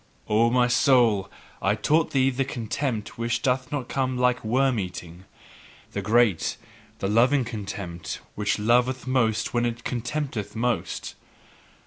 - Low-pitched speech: Yes, low, 120 Hz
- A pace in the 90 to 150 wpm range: Yes, slow, 135 wpm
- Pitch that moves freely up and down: No, average, 3.1 semitones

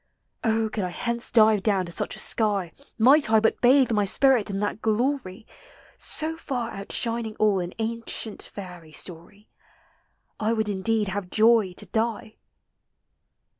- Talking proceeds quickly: No, average, 150 wpm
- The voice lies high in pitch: Yes, high, 220 Hz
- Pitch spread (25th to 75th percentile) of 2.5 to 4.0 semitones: Yes, average, 2.8 semitones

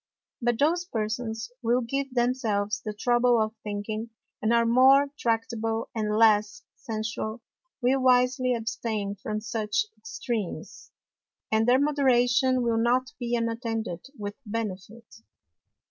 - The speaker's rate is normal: No, slow, 125 wpm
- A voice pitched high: Yes, high, 230 Hz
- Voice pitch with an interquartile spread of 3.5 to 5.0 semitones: No, narrow, 2.5 semitones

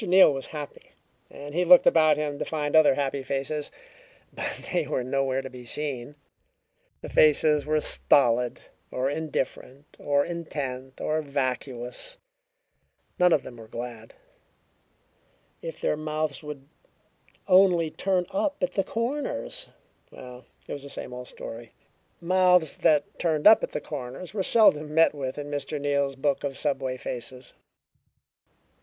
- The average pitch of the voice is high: No, medium, 145 Hz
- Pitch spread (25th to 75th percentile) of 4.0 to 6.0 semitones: No, average, 3.3 semitones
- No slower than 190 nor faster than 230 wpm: No, average, 145 wpm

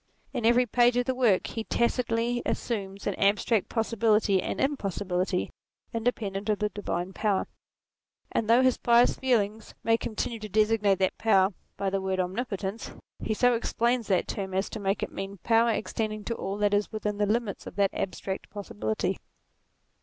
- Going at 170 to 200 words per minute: Yes, average, 175 wpm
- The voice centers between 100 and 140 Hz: No, high, 215 Hz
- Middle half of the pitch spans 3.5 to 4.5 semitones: No, average, 2.9 semitones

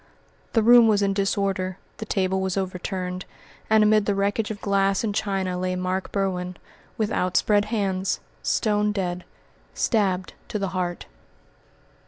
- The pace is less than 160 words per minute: Yes, average, 145 wpm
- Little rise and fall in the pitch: Yes, narrow, 2.1 semitones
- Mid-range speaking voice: No, high, 195 Hz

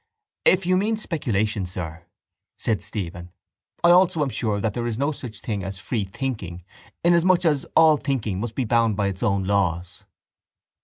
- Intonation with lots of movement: Yes, wide, 7.4 semitones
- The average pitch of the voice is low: Yes, low, 110 Hz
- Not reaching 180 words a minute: Yes, average, 170 wpm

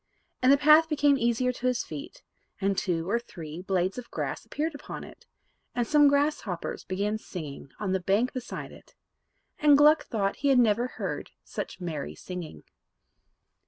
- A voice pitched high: Yes, high, 230 Hz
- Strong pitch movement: Yes, wide, 7.2 semitones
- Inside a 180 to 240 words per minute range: No, average, 165 wpm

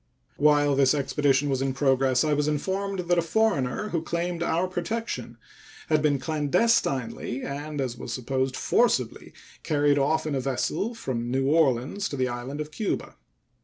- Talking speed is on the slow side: No, average, 165 wpm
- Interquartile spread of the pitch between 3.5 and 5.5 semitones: Yes, average, 4.0 semitones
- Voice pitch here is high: No, medium, 145 Hz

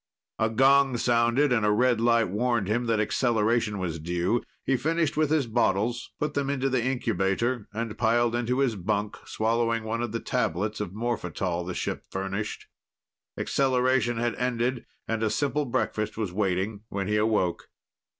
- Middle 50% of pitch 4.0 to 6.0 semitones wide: No, average, 3.0 semitones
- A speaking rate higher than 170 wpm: No, average, 165 wpm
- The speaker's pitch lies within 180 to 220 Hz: No, low, 115 Hz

